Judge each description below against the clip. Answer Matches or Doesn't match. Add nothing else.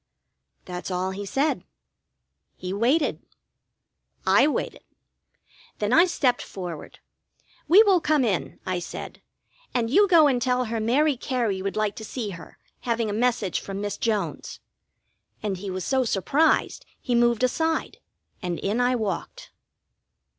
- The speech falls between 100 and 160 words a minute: Matches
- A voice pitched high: Matches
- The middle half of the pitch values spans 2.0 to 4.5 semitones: Doesn't match